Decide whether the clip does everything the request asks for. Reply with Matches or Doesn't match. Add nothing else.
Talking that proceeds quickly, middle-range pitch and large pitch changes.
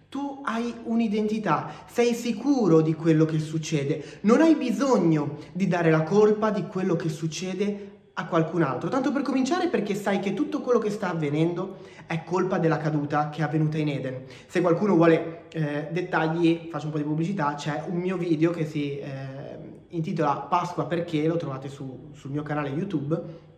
Doesn't match